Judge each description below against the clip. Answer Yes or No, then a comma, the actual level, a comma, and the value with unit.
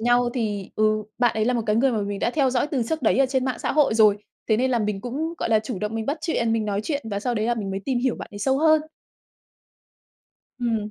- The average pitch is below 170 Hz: No, high, 235 Hz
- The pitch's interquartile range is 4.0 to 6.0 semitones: No, average, 3.5 semitones